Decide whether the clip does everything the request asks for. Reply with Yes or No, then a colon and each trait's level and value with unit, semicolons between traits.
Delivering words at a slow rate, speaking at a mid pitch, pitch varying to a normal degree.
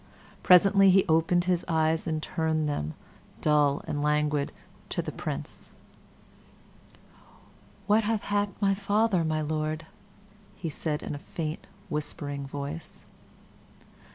Yes: slow, 120 wpm; medium, 160 Hz; average, 3.7 semitones